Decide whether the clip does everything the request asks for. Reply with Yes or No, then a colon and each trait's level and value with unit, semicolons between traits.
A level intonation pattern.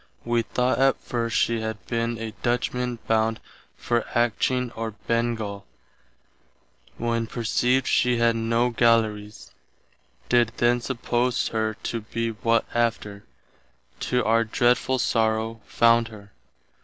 Yes: narrow, 1.3 semitones